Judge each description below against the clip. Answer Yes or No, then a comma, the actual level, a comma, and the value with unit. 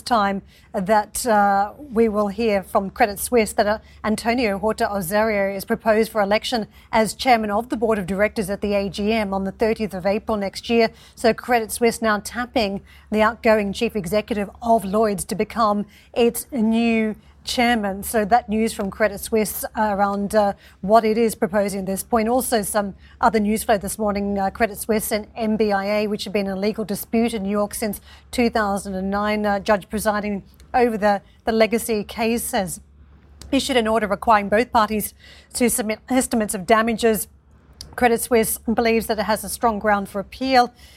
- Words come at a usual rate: Yes, average, 175 wpm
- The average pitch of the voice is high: Yes, high, 220 Hz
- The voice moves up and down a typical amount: No, narrow, 2.0 semitones